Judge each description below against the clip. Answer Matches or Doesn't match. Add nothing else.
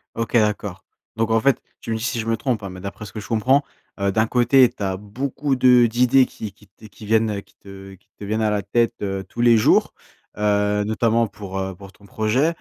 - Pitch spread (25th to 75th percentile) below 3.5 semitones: Matches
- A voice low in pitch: Matches